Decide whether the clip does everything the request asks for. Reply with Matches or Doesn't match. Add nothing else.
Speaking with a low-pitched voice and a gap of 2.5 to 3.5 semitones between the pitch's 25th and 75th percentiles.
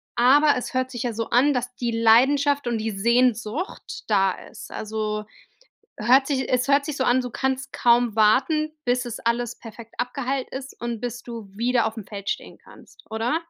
Doesn't match